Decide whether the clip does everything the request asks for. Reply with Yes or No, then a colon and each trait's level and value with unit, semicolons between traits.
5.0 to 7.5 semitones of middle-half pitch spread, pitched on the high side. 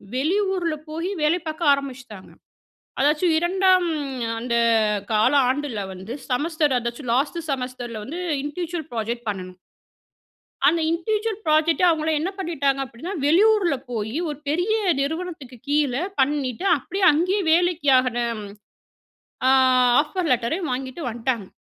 Yes: wide, 5.6 semitones; very high, 295 Hz